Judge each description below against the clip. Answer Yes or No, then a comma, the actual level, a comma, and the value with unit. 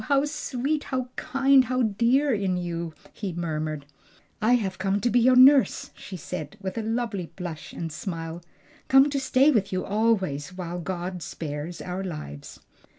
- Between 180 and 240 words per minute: No, average, 165 wpm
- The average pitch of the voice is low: No, high, 195 Hz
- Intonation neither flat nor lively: No, wide, 6.6 semitones